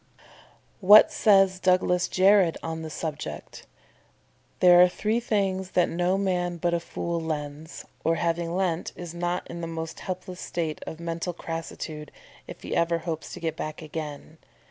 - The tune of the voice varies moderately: No, narrow, 2.1 semitones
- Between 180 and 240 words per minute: No, average, 160 wpm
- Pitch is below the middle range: No, medium, 170 Hz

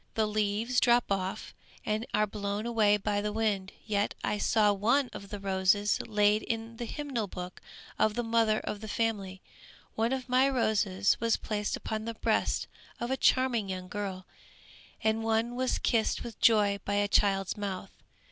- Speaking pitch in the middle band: No, high, 215 Hz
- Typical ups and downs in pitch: No, narrow, 2.2 semitones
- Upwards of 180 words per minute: No, average, 175 wpm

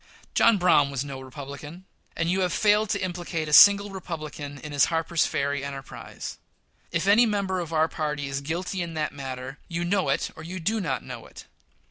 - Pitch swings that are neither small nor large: Yes, average, 4.6 semitones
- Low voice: No, medium, 160 Hz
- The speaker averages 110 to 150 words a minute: No, average, 195 wpm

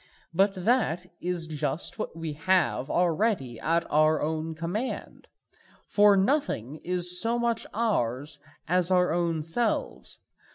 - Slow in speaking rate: Yes, slow, 125 wpm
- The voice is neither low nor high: Yes, medium, 175 Hz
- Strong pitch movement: No, average, 4.4 semitones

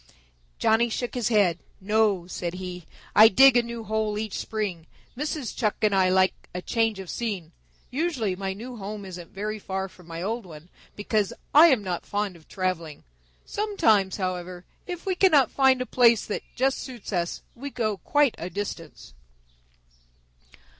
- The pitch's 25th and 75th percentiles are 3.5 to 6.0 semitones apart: Yes, average, 4.5 semitones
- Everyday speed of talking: Yes, average, 165 wpm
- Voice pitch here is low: No, high, 210 Hz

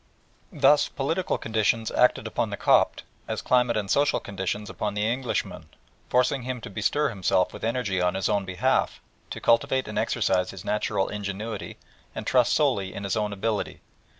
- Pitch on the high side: No, low, 105 Hz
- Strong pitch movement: No, average, 4.0 semitones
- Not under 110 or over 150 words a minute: No, average, 170 wpm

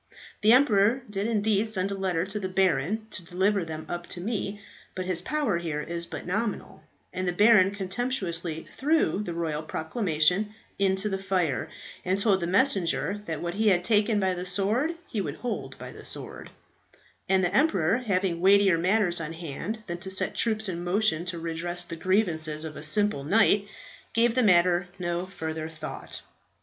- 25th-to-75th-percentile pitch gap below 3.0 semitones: No, average, 3.4 semitones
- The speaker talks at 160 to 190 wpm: Yes, average, 180 wpm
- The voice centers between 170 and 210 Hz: Yes, high, 190 Hz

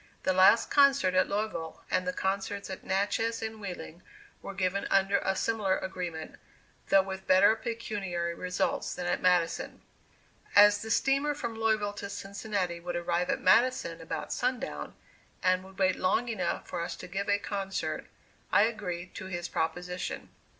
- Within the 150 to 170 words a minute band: Yes, average, 160 wpm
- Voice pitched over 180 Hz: Yes, high, 190 Hz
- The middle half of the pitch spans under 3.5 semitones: Yes, average, 3.0 semitones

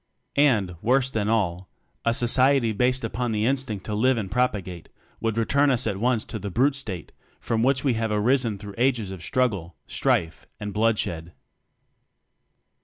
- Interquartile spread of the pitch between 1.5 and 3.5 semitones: No, average, 3.9 semitones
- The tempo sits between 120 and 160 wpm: No, average, 170 wpm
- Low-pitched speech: Yes, low, 115 Hz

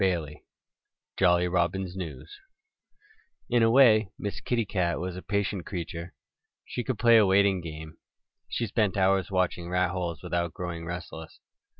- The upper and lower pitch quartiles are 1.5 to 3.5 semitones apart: Yes, average, 2.8 semitones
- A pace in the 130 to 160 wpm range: Yes, average, 145 wpm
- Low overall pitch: Yes, very low, 90 Hz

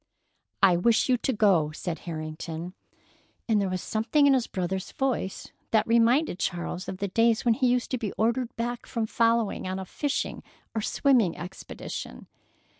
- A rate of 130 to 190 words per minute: Yes, average, 170 wpm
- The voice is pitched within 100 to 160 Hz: No, high, 220 Hz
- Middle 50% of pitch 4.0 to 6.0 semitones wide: Yes, average, 4.6 semitones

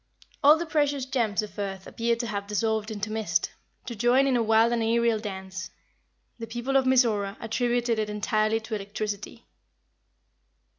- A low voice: No, high, 225 Hz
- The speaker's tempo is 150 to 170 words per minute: Yes, average, 160 wpm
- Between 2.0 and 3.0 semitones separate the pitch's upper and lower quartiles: Yes, narrow, 2.4 semitones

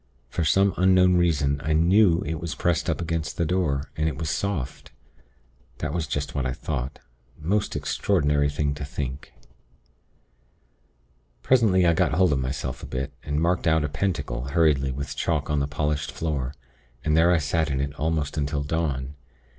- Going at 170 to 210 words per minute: Yes, average, 175 wpm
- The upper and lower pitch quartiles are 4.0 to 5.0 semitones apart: No, average, 3.0 semitones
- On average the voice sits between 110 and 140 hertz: No, very low, 75 Hz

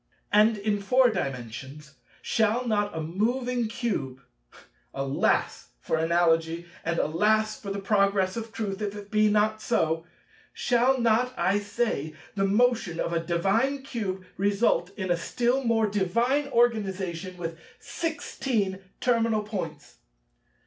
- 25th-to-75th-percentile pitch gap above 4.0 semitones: Yes, average, 5.1 semitones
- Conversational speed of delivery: No, slow, 125 wpm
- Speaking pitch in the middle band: No, high, 205 Hz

